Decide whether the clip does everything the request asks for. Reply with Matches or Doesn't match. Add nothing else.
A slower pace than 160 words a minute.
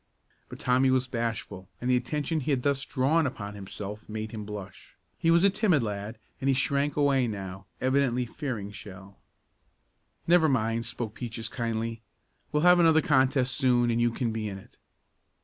Doesn't match